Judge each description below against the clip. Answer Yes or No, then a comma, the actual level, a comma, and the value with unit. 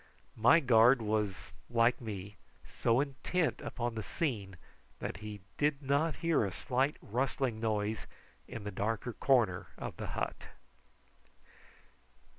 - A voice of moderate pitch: No, low, 115 Hz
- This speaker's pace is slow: Yes, slow, 125 wpm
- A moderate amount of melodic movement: Yes, average, 4.4 semitones